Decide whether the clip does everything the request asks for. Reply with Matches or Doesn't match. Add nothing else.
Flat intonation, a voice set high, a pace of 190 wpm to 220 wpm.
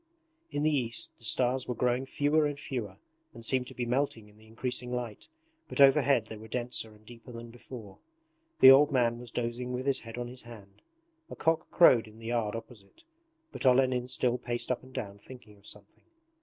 Doesn't match